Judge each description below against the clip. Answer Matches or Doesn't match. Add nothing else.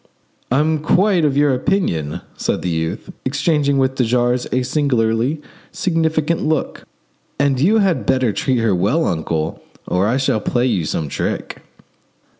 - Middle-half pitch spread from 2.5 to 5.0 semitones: Doesn't match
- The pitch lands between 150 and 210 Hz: Doesn't match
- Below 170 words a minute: Matches